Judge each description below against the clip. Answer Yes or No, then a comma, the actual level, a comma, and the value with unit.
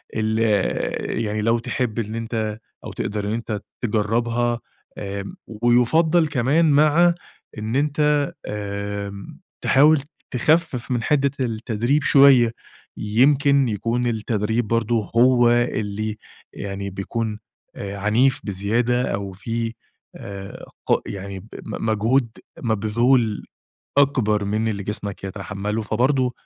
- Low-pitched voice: Yes, low, 115 Hz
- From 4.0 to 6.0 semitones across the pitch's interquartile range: No, average, 3.3 semitones